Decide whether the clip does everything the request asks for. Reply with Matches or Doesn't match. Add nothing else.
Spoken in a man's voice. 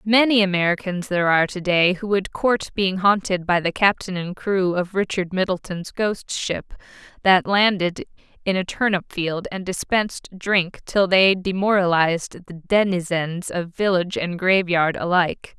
Doesn't match